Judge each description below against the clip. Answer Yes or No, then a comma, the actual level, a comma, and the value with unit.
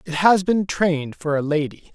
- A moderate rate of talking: No, fast, 215 wpm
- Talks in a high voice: No, medium, 165 Hz